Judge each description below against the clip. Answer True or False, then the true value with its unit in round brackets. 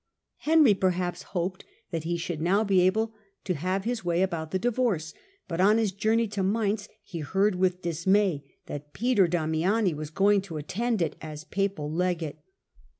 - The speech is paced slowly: False (170 wpm)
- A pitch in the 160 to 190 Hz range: True (185 Hz)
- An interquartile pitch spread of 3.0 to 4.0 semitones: True (3.7 semitones)